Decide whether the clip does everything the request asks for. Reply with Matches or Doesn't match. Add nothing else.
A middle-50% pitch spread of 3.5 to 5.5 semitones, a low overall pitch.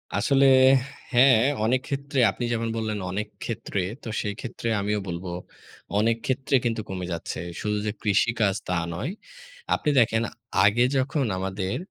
Matches